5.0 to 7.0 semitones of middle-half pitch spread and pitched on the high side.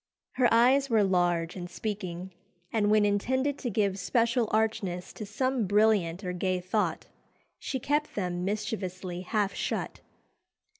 No: average, 3.8 semitones; high, 205 Hz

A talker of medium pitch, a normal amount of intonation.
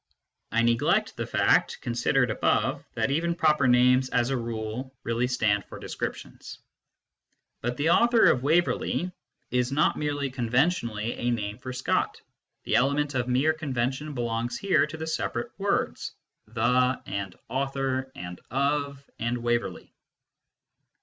No: low, 130 Hz; average, 3.4 semitones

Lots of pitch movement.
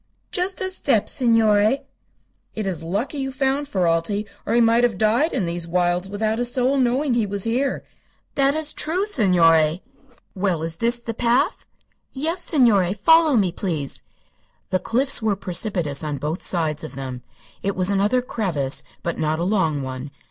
Yes: wide, 6.7 semitones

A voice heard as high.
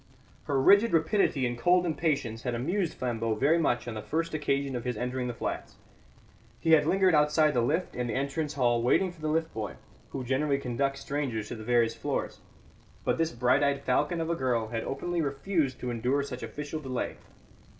No: medium, 140 Hz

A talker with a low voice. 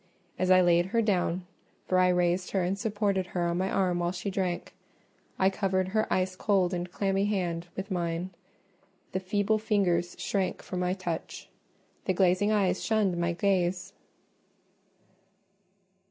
No: medium, 185 Hz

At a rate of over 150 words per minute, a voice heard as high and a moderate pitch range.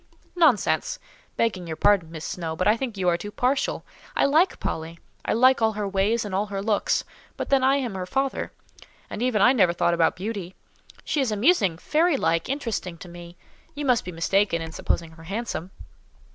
No: average, 185 wpm; high, 205 Hz; wide, 6.6 semitones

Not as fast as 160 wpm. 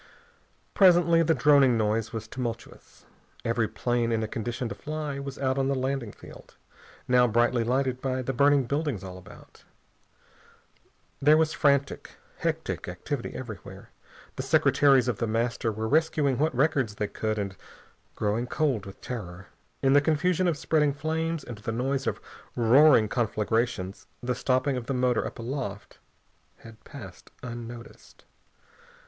Yes: average, 150 wpm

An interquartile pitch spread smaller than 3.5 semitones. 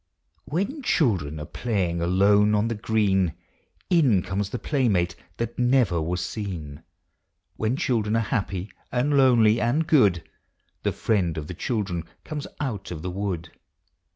No: wide, 5.4 semitones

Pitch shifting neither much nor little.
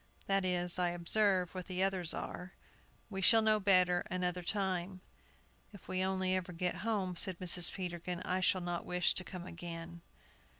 No: narrow, 1.4 semitones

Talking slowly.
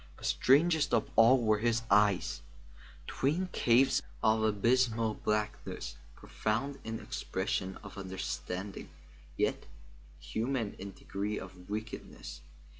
Yes: slow, 110 wpm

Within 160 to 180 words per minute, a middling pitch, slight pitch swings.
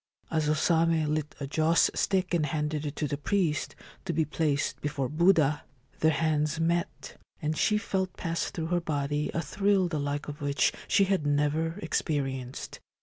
Yes: average, 175 wpm; medium, 155 Hz; narrow, 2.3 semitones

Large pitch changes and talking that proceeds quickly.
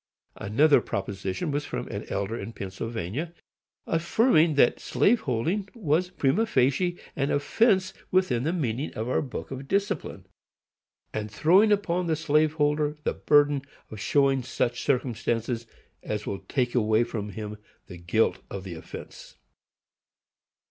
No: wide, 6.8 semitones; slow, 135 wpm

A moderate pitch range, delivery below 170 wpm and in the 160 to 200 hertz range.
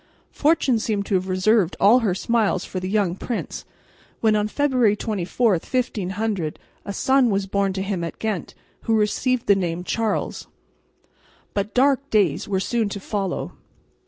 No: average, 3.2 semitones; average, 160 wpm; high, 210 Hz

